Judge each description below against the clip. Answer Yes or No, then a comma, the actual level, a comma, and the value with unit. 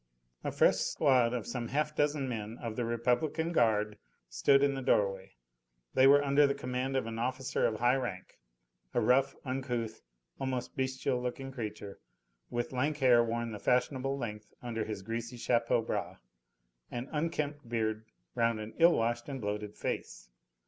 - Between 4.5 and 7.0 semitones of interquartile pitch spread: No, average, 3.1 semitones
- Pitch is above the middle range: No, low, 125 Hz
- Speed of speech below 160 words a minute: No, average, 165 wpm